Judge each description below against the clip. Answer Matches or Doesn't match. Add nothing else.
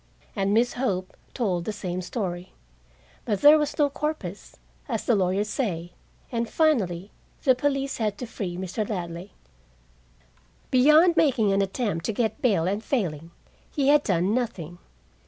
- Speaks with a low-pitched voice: Doesn't match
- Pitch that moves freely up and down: Matches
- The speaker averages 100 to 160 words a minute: Matches